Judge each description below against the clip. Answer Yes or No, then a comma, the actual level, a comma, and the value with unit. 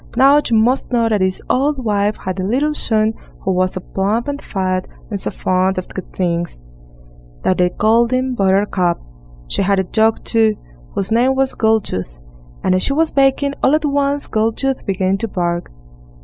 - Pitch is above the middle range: Yes, high, 215 Hz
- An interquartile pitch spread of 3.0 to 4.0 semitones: No, wide, 5.6 semitones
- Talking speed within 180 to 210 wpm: Yes, average, 185 wpm